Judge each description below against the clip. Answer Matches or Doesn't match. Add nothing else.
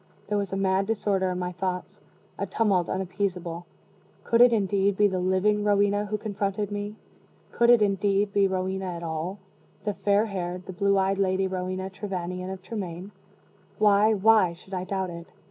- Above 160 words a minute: Matches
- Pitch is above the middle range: Matches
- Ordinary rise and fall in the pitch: Doesn't match